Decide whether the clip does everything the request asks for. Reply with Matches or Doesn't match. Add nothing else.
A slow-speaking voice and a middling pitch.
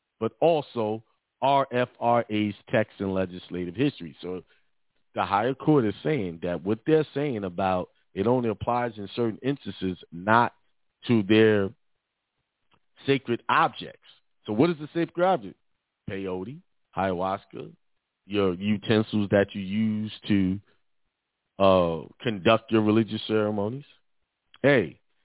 Doesn't match